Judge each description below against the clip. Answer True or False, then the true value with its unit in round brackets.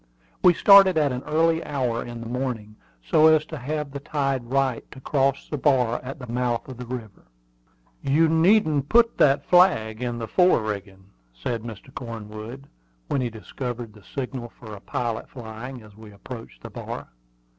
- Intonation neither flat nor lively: True (4.0 semitones)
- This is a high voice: False (125 Hz)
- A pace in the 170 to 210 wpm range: True (175 wpm)